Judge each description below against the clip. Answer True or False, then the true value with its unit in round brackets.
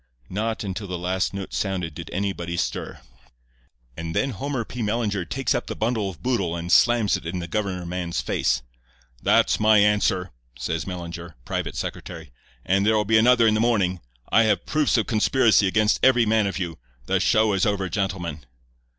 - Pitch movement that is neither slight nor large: True (3.8 semitones)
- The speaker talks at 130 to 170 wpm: False (180 wpm)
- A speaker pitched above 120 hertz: False (100 Hz)